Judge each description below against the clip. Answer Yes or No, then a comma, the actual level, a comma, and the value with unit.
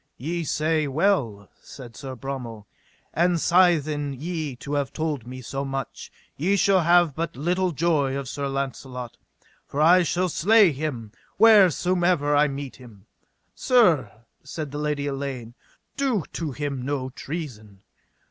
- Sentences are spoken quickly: No, average, 140 wpm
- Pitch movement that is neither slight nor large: Yes, average, 4.4 semitones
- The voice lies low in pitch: No, medium, 145 Hz